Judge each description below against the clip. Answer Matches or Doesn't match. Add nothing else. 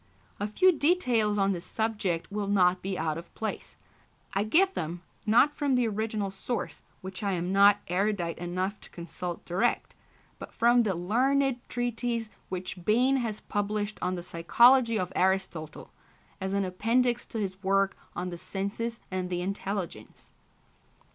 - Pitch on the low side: Doesn't match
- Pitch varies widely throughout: Doesn't match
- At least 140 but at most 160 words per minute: Matches